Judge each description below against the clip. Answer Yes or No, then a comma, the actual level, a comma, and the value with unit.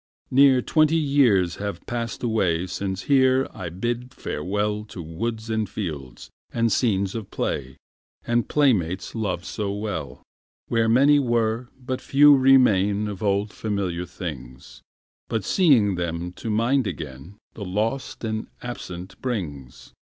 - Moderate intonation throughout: Yes, average, 5.0 semitones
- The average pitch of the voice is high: No, low, 105 Hz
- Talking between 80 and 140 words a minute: Yes, slow, 135 wpm